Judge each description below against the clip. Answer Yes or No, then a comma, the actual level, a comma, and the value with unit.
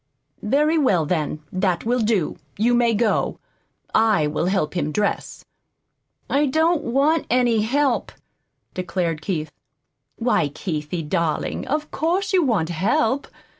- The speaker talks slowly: Yes, slow, 130 wpm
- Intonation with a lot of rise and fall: Yes, wide, 8.0 semitones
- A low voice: No, high, 215 Hz